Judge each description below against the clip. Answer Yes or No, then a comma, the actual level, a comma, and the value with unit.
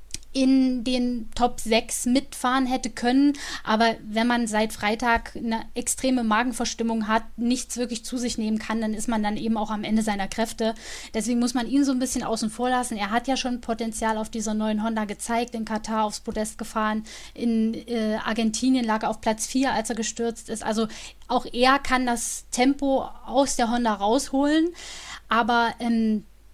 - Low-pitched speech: No, high, 230 Hz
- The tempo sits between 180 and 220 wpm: Yes, average, 185 wpm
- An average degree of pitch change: No, narrow, 2.1 semitones